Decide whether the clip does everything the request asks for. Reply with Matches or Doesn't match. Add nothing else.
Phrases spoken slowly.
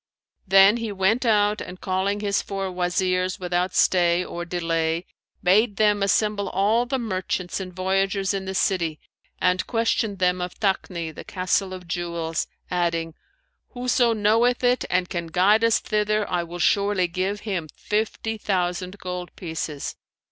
Doesn't match